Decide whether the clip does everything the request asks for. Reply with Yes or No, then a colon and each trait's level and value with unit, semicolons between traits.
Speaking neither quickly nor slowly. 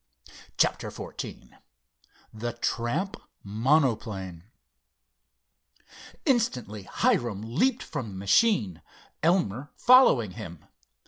No: slow, 75 wpm